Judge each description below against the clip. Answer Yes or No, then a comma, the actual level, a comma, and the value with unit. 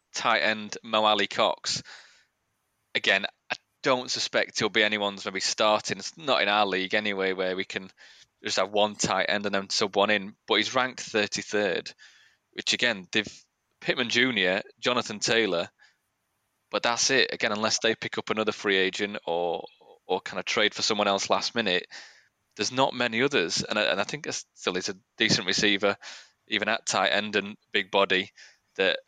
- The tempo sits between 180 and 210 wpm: Yes, average, 190 wpm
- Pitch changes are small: Yes, narrow, 1.6 semitones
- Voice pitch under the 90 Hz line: No, low, 100 Hz